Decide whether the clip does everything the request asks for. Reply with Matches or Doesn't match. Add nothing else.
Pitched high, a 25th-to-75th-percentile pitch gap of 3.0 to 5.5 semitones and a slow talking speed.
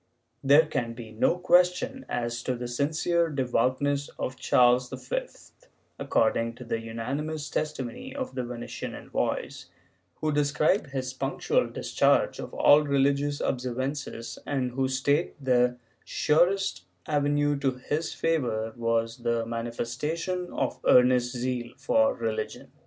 Doesn't match